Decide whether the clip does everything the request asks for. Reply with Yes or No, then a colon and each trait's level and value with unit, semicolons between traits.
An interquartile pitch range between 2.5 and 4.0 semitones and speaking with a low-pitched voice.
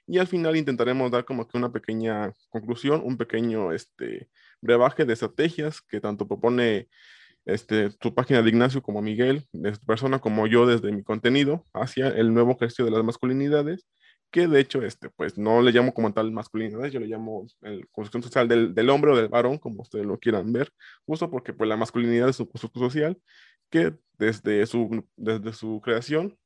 Yes: average, 3.0 semitones; low, 120 Hz